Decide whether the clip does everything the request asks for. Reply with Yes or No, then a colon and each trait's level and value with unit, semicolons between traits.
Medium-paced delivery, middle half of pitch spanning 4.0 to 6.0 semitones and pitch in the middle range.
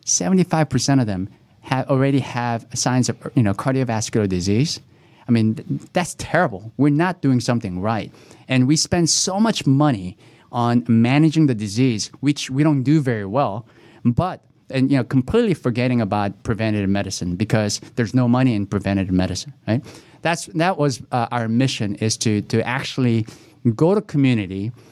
No: average, 160 wpm; average, 4.6 semitones; low, 125 Hz